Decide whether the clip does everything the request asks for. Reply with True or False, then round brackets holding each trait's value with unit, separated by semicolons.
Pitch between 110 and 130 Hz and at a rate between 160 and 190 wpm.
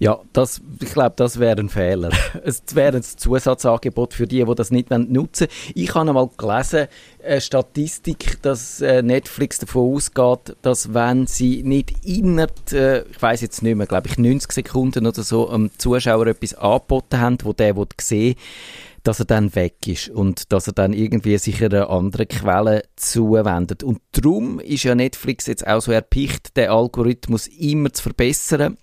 True (120 Hz; 175 wpm)